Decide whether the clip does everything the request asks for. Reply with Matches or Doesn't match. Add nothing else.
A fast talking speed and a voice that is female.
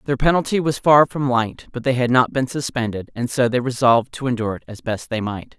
Matches